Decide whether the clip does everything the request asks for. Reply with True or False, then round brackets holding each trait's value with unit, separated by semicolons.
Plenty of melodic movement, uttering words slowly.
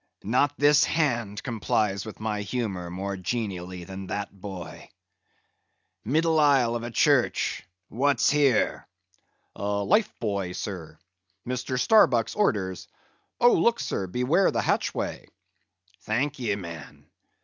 True (6.0 semitones; 115 wpm)